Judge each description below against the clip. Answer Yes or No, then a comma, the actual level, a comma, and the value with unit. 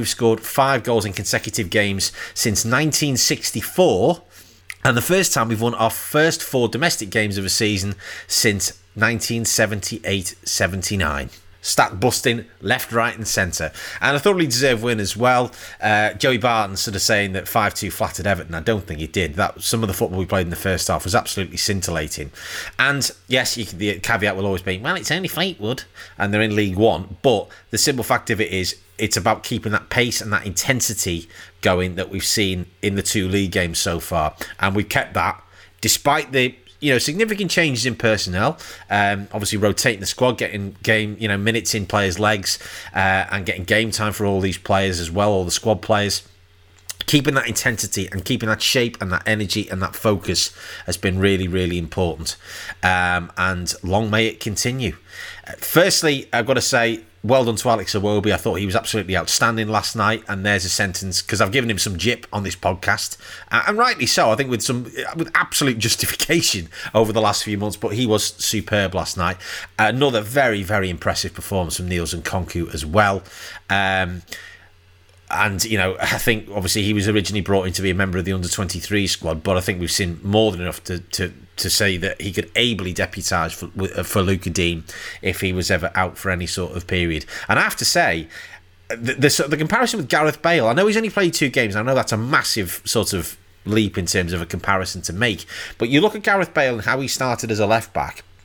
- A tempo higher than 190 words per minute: Yes, fast, 205 wpm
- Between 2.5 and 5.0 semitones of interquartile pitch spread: Yes, average, 3.5 semitones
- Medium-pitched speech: No, low, 105 Hz